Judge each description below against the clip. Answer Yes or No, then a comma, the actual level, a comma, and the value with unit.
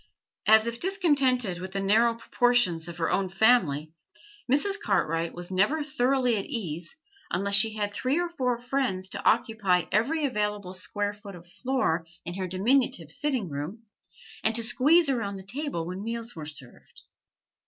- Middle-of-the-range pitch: No, high, 210 Hz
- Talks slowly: No, average, 165 wpm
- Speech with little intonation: No, wide, 5.4 semitones